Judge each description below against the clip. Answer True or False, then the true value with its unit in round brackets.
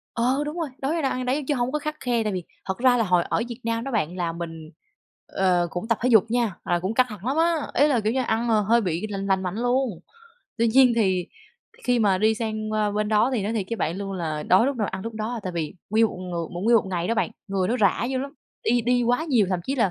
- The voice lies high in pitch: True (220 Hz)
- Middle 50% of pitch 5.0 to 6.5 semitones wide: False (4.5 semitones)